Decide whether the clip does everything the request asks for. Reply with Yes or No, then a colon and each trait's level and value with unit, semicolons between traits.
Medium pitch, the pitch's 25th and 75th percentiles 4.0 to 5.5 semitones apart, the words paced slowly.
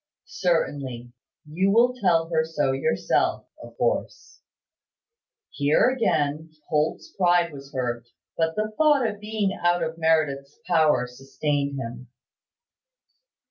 Yes: medium, 160 Hz; average, 5.2 semitones; slow, 115 wpm